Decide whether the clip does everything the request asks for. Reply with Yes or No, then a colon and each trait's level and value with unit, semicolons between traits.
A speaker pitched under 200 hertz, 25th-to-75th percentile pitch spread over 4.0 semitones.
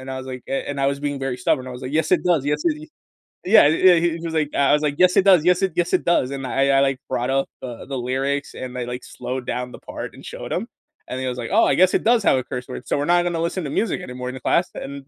Yes: medium, 140 Hz; average, 4.8 semitones